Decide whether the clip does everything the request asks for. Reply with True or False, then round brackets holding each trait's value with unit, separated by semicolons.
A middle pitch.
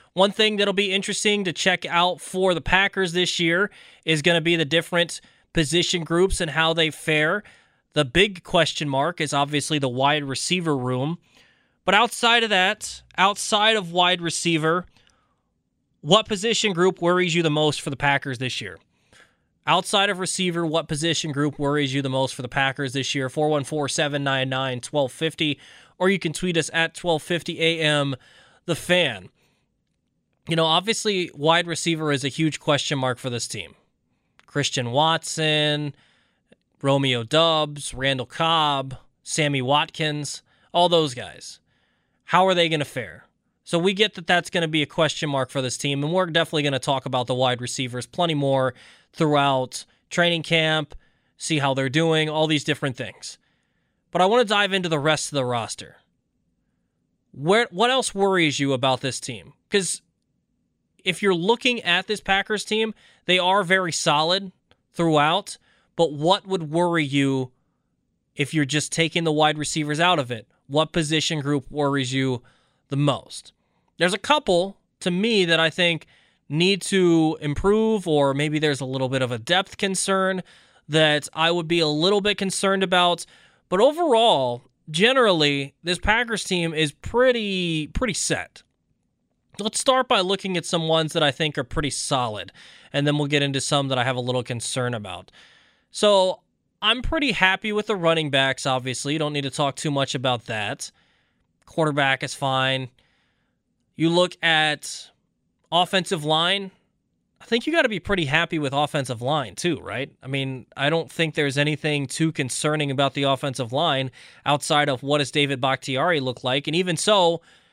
True (155 Hz)